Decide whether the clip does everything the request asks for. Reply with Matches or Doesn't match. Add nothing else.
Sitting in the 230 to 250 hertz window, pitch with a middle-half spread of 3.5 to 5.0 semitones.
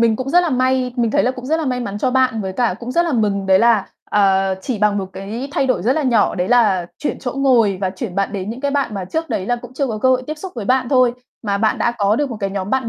Matches